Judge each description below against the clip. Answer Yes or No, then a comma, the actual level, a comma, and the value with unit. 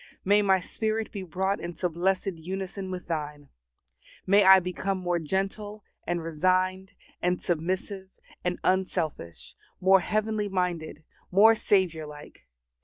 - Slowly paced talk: Yes, slow, 125 wpm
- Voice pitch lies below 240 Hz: Yes, medium, 185 Hz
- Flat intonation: Yes, narrow, 2.2 semitones